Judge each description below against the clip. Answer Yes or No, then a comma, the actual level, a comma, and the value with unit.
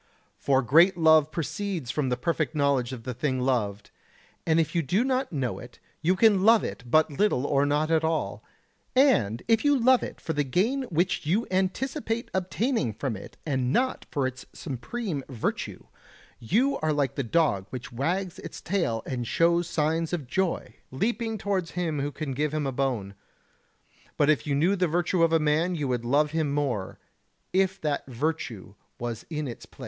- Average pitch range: No, wide, 5.8 semitones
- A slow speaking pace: No, average, 185 wpm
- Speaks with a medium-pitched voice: Yes, medium, 155 Hz